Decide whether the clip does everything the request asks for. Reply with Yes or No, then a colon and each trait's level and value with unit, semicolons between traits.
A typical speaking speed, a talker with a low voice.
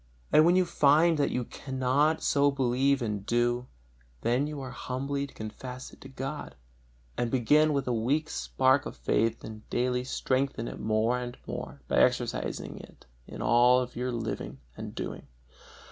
Yes: average, 170 wpm; low, 130 Hz